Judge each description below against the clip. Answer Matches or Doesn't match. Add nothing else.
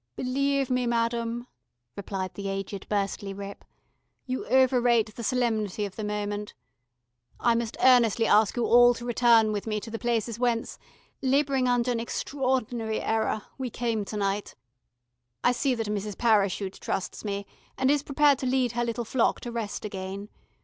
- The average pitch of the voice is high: Matches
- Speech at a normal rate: Matches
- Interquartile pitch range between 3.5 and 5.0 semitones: Doesn't match